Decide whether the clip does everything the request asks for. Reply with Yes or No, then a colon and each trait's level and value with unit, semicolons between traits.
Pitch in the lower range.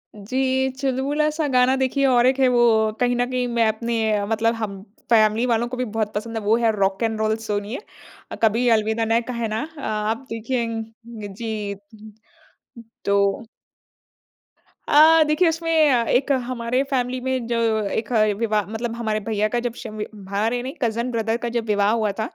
No: high, 230 Hz